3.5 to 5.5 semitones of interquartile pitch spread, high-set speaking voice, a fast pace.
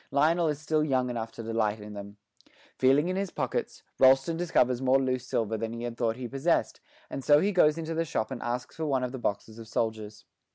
No: average, 5.1 semitones; low, 130 Hz; fast, 230 wpm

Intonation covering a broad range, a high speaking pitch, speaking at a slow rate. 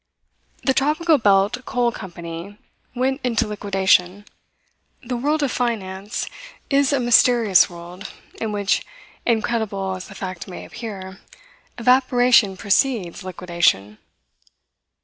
No: average, 4.7 semitones; high, 210 Hz; slow, 110 wpm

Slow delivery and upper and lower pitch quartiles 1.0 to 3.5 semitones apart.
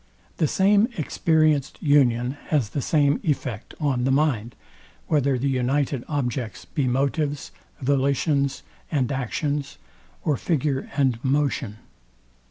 Yes: slow, 115 wpm; narrow, 2.6 semitones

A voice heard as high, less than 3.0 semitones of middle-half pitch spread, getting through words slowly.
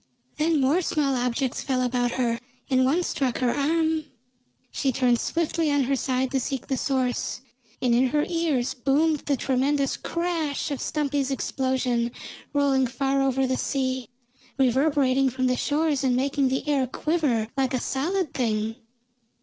No: very high, 270 Hz; narrow, 2.4 semitones; average, 160 wpm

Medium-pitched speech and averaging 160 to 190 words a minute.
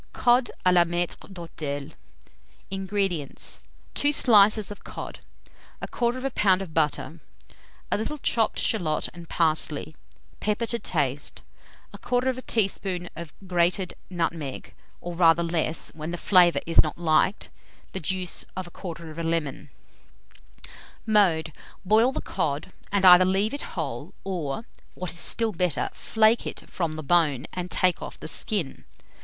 No: medium, 180 Hz; slow, 135 wpm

